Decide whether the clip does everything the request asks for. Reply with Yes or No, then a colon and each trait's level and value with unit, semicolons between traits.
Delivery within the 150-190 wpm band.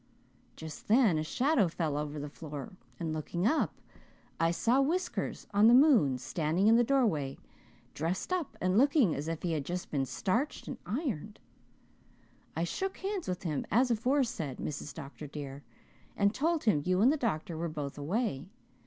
Yes: average, 170 wpm